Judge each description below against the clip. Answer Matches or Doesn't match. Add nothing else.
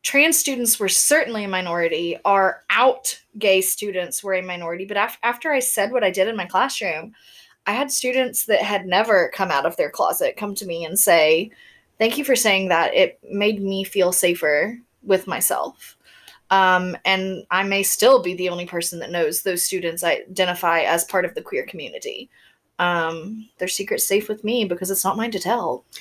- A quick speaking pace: Doesn't match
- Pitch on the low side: Doesn't match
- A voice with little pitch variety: Doesn't match